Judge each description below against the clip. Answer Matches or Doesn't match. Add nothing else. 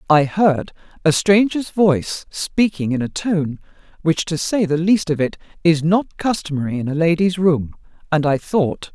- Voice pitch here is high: Doesn't match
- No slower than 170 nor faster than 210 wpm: Matches